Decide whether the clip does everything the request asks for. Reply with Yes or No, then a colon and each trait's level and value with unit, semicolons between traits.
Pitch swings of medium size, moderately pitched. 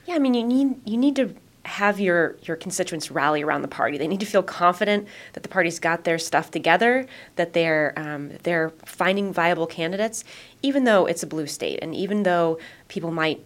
Yes: average, 4.3 semitones; medium, 175 Hz